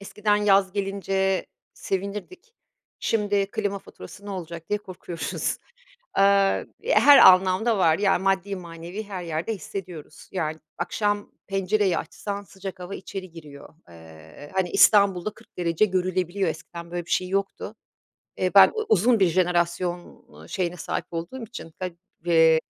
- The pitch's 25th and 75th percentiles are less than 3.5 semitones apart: Yes, average, 2.7 semitones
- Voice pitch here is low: No, high, 190 Hz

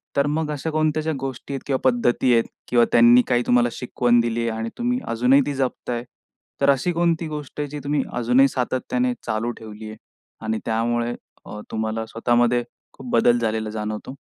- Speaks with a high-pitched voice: No, low, 120 Hz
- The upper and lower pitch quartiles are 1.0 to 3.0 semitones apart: No, average, 3.6 semitones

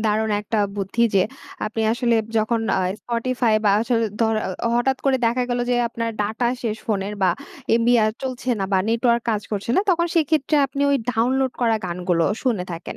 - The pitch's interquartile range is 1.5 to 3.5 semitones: Yes, average, 2.9 semitones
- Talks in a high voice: Yes, high, 230 Hz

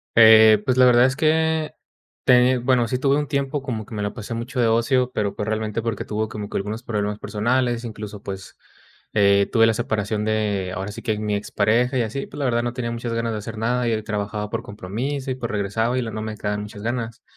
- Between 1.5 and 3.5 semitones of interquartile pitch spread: Yes, average, 2.9 semitones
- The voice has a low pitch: Yes, low, 115 Hz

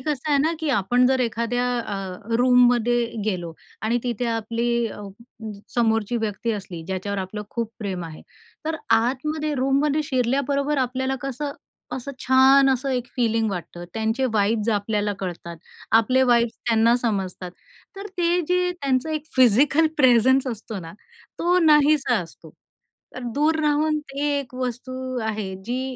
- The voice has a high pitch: Yes, high, 245 Hz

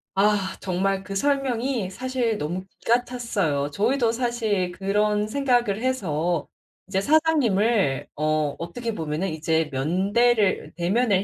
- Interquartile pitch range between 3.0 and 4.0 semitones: No, average, 5.3 semitones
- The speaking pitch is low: No, high, 200 Hz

